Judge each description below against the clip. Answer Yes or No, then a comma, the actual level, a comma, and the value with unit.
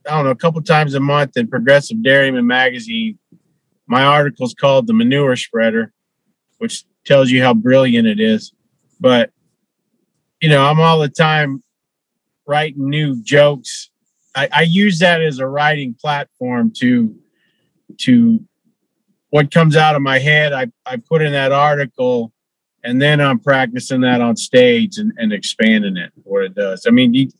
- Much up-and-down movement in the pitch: Yes, wide, 8.2 semitones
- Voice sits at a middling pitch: Yes, medium, 150 Hz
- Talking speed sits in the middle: Yes, average, 160 wpm